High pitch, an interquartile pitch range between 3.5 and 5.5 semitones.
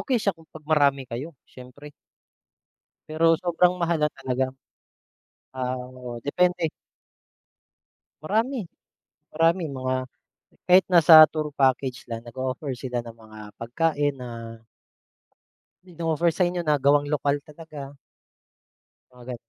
No: medium, 145 Hz; average, 4.4 semitones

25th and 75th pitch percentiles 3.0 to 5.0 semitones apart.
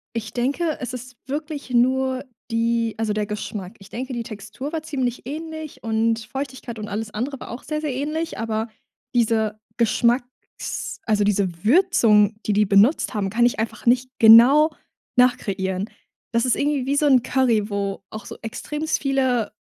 Yes: average, 3.8 semitones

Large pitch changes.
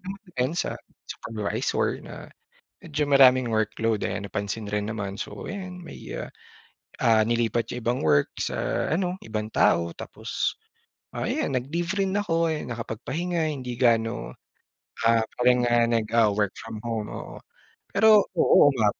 Yes: wide, 6.1 semitones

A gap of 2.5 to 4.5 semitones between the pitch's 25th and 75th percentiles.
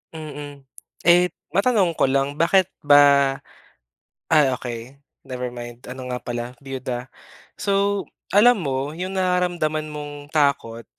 No: average, 5.2 semitones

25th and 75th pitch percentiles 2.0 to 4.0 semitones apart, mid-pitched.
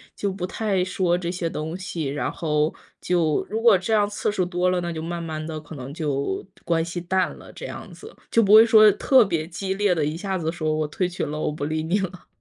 Yes: average, 3.5 semitones; medium, 175 Hz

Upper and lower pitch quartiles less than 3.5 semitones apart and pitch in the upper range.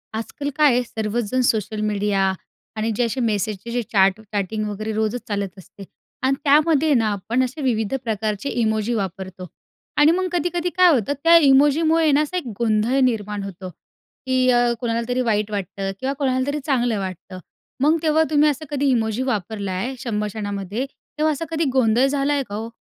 No: average, 5.1 semitones; high, 235 Hz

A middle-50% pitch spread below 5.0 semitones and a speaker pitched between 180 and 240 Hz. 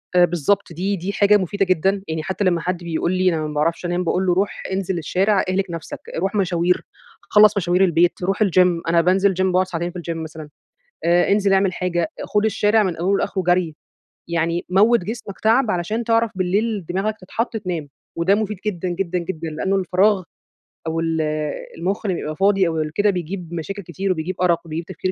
Yes: average, 2.8 semitones; medium, 185 Hz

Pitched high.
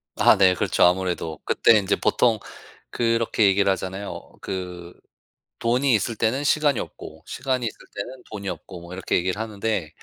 No: low, 100 Hz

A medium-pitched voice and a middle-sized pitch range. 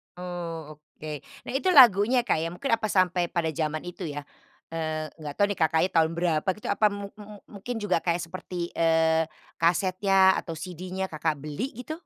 Yes: medium, 175 Hz; average, 3.5 semitones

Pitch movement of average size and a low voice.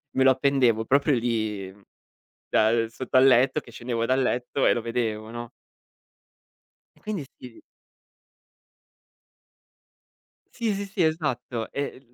Yes: average, 3.2 semitones; low, 125 Hz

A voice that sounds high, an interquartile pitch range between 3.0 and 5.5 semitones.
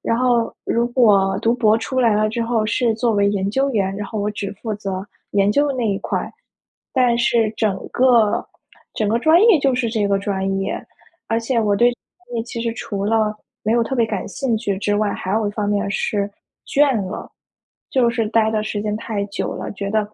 No: high, 220 Hz; narrow, 2.6 semitones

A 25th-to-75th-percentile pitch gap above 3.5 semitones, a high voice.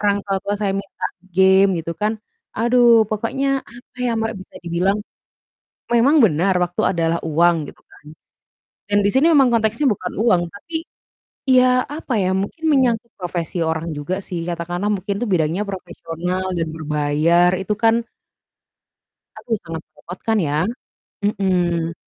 Yes: average, 5.0 semitones; high, 195 Hz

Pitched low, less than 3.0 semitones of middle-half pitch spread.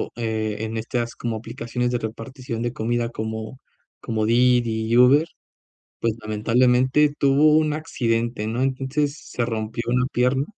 Yes: low, 120 Hz; narrow, 2.5 semitones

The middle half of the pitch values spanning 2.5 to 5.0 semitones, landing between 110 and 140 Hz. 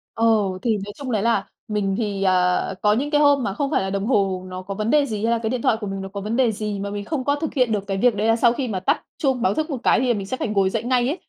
No: average, 4.3 semitones; high, 220 Hz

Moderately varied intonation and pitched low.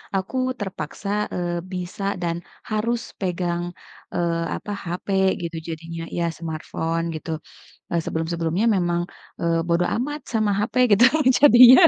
No: average, 3.6 semitones; medium, 175 Hz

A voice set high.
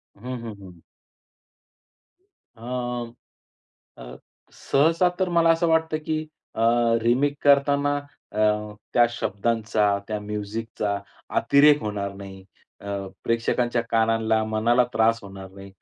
No: low, 115 Hz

